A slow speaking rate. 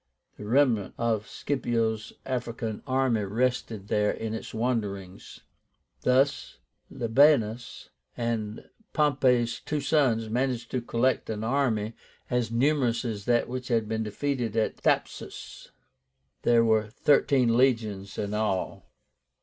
Yes: slow, 115 wpm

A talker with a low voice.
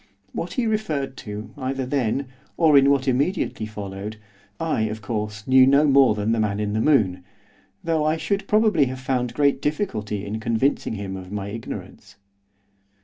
Yes: low, 130 Hz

